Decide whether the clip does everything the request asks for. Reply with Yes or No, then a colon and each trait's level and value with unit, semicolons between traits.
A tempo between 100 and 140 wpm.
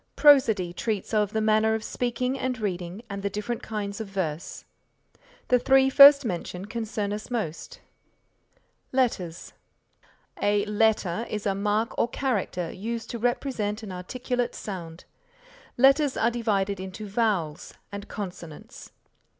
Yes: slow, 135 wpm